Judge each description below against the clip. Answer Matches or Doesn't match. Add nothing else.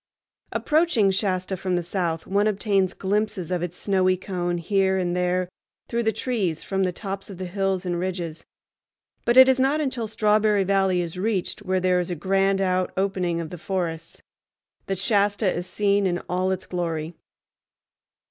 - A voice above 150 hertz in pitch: Matches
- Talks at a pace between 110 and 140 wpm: Doesn't match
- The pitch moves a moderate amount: Doesn't match